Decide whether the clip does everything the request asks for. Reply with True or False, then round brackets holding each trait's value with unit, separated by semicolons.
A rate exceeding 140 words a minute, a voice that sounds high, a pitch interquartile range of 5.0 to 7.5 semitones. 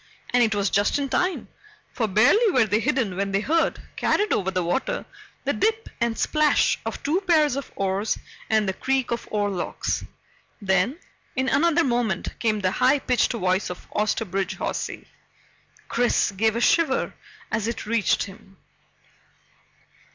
True (155 wpm; 225 Hz; 5.5 semitones)